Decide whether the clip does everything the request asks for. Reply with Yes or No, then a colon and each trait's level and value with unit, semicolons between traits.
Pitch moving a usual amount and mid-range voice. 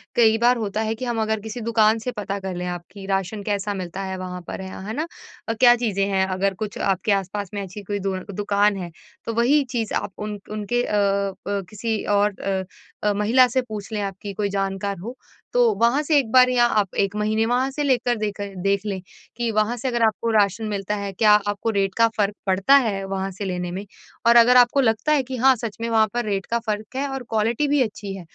No: average, 3.1 semitones; high, 210 Hz